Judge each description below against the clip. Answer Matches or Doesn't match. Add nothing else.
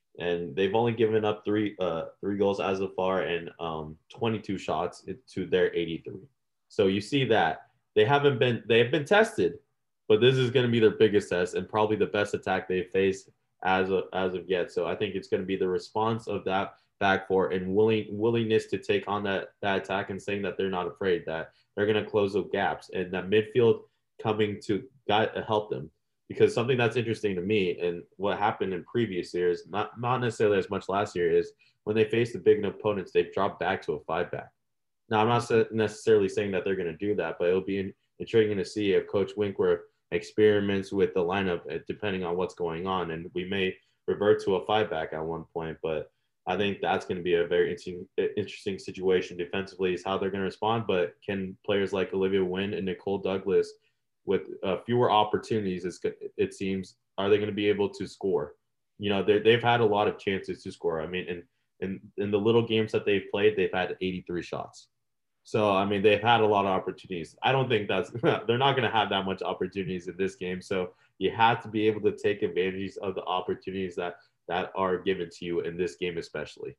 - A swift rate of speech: Matches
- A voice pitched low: Matches